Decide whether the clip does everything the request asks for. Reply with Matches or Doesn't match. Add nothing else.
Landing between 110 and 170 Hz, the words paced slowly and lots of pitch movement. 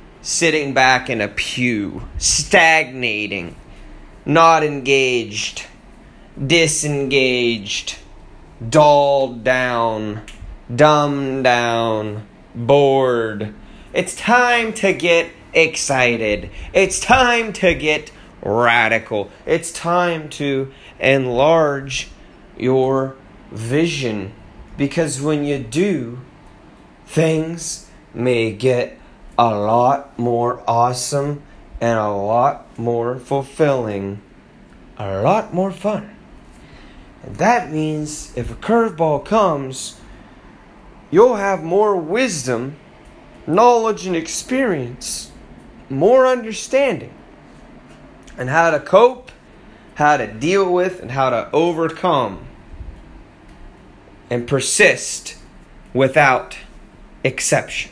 Matches